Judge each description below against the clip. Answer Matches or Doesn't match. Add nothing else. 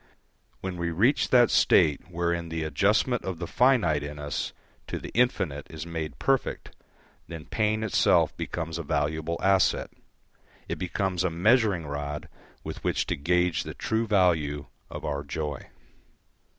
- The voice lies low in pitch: Matches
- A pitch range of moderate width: Matches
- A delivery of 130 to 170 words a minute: Matches